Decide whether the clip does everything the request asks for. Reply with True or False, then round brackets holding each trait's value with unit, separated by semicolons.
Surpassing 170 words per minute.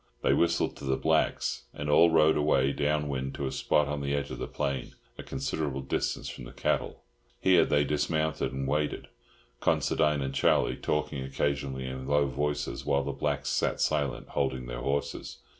True (180 wpm)